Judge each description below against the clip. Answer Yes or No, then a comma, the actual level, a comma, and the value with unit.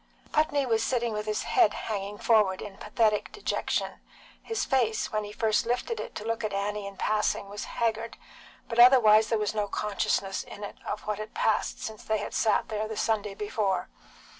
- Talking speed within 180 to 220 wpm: Yes, average, 190 wpm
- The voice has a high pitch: Yes, high, 215 Hz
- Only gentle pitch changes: Yes, narrow, 1.7 semitones